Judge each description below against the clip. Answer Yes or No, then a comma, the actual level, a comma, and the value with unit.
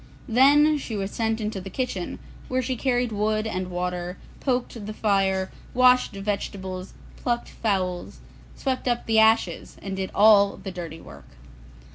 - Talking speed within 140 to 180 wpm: Yes, average, 150 wpm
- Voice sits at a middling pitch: No, high, 210 Hz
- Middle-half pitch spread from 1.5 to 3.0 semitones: No, average, 4.3 semitones